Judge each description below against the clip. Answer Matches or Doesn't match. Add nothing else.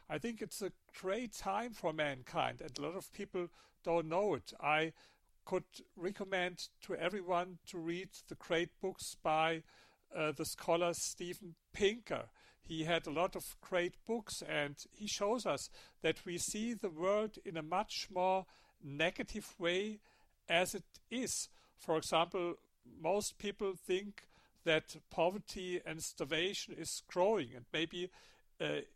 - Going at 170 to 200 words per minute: Doesn't match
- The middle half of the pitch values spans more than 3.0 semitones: Matches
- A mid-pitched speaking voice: Matches